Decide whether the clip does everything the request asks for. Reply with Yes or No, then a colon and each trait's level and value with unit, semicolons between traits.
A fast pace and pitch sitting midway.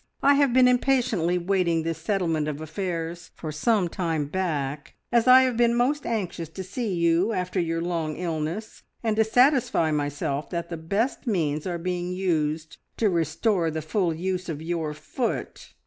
No: average, 170 wpm; medium, 175 Hz